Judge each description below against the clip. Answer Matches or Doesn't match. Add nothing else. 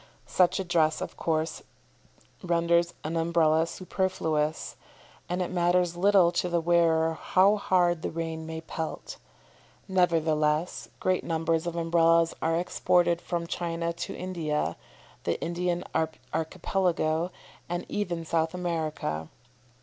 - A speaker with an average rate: Doesn't match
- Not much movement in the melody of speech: Matches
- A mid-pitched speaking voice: Matches